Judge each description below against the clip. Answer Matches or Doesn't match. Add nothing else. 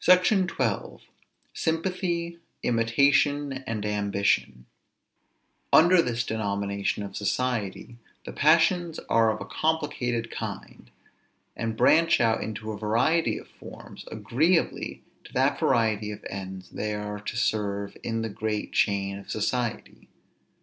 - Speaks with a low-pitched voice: Matches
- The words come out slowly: Matches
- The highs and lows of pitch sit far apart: Matches